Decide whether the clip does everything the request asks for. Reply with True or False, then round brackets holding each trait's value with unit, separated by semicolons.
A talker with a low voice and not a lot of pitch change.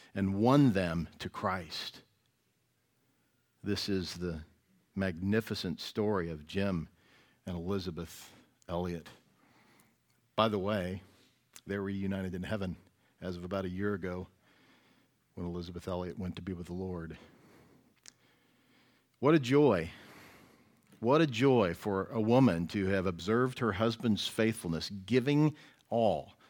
False (95 Hz; 3.8 semitones)